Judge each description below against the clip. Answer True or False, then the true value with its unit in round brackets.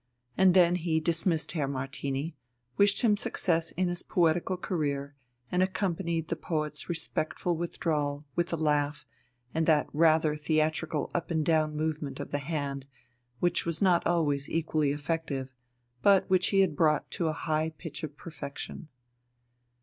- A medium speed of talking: True (150 wpm)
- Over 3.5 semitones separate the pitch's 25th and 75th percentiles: False (2.5 semitones)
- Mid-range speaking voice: True (160 Hz)